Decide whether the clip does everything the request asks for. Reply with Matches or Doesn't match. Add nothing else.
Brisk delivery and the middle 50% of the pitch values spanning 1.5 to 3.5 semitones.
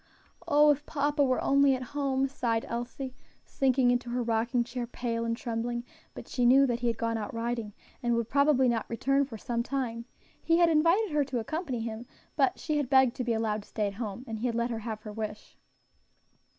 Matches